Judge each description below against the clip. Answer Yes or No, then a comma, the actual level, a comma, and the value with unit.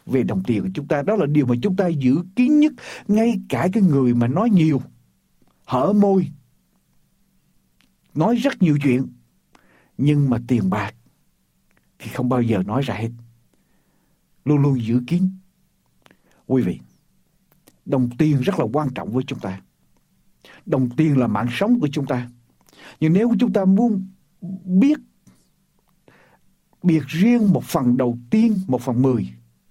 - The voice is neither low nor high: Yes, medium, 145 Hz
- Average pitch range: No, wide, 7.6 semitones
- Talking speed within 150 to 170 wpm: Yes, fast, 155 wpm